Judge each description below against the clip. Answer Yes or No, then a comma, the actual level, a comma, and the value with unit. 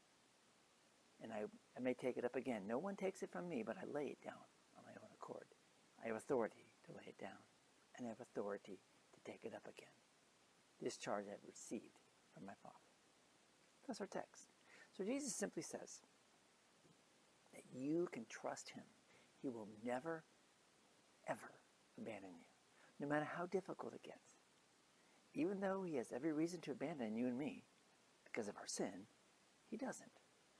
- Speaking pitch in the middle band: Yes, medium, 165 Hz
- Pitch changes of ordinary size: No, wide, 6.5 semitones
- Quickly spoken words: No, average, 165 wpm